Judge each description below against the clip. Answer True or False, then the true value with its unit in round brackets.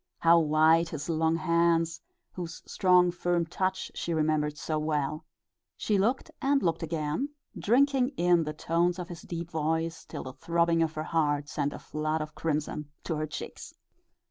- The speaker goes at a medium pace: True (170 wpm)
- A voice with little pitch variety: True (2.1 semitones)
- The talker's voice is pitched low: False (165 Hz)